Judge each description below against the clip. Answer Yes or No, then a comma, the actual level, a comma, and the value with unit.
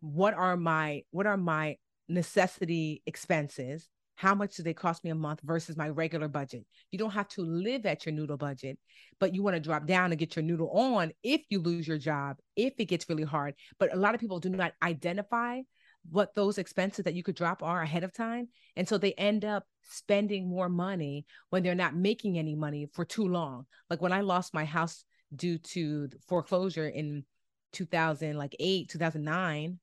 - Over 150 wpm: Yes, average, 200 wpm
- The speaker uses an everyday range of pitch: Yes, average, 3.6 semitones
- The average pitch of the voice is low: No, medium, 170 Hz